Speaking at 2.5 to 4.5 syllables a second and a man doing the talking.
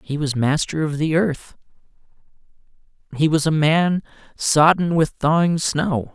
Yes: 4.1 syllables/s; male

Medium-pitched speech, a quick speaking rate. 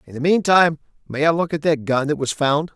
Yes: medium, 150 Hz; fast, 260 wpm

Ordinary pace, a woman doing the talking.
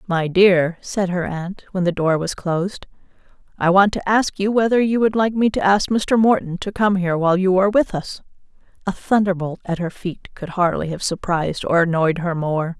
No: fast, 210 wpm; female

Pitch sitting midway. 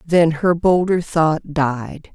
Yes: medium, 160 Hz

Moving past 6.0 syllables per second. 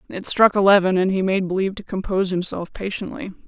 Yes: 6.3 syllables/s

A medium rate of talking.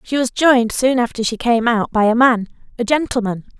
No: fast, 215 wpm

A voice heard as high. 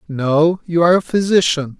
No: medium, 165 Hz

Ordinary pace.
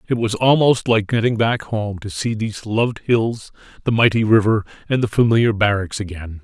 Yes: average, 185 wpm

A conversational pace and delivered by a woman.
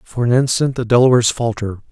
No: average, 190 wpm; male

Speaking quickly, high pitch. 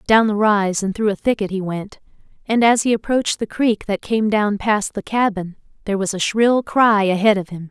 Yes: fast, 225 wpm; high, 210 Hz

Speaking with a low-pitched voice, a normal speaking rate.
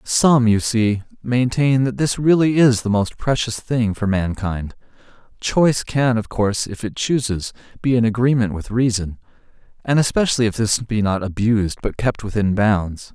Yes: low, 115 Hz; average, 170 wpm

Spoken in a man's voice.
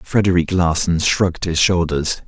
Yes: male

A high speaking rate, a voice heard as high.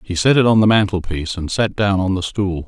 No: fast, 270 wpm; very low, 95 Hz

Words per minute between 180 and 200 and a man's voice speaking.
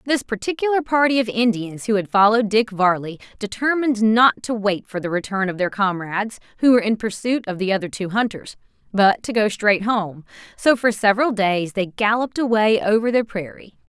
No: average, 190 wpm; female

